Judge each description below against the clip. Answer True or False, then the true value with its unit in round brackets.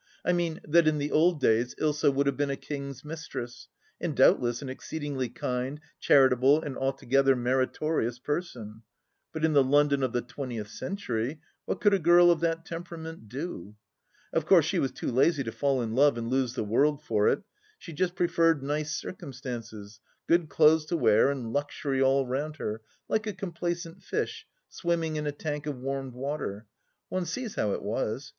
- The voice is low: False (145 Hz)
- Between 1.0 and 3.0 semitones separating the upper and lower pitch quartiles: False (4.3 semitones)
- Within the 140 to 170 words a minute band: False (185 wpm)